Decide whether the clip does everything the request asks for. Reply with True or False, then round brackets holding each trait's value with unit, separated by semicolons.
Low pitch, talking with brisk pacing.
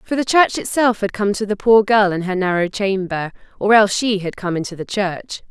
False (200 Hz; 240 wpm)